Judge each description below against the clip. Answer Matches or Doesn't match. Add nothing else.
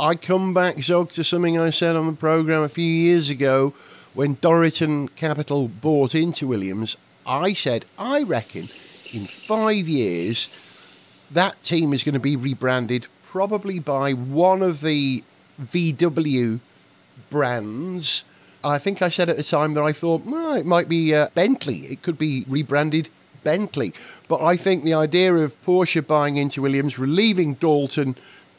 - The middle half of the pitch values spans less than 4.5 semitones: Matches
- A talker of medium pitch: Matches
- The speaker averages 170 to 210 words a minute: Doesn't match